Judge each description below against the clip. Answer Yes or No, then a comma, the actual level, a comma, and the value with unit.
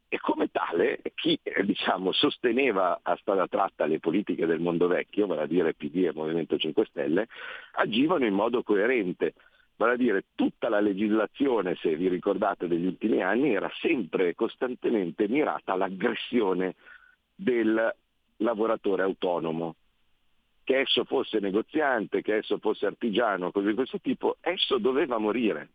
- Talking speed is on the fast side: No, average, 145 wpm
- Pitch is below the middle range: No, very high, 270 Hz